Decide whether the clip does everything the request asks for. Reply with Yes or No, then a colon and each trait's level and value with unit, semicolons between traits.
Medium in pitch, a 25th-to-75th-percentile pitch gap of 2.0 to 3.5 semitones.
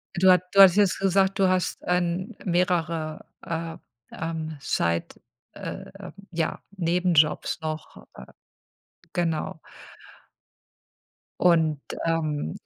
Yes: medium, 170 Hz; narrow, 2.5 semitones